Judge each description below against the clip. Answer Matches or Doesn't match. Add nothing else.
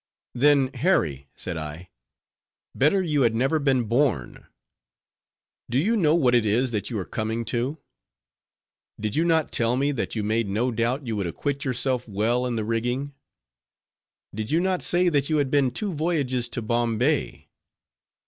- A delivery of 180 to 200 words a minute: Doesn't match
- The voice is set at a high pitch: Doesn't match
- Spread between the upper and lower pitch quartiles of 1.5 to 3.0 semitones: Doesn't match